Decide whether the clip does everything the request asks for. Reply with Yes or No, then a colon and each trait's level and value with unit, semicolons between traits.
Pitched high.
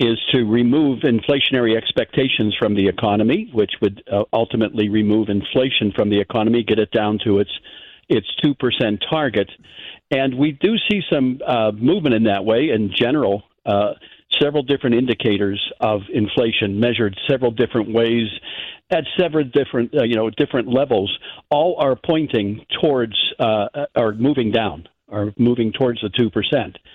No: low, 115 Hz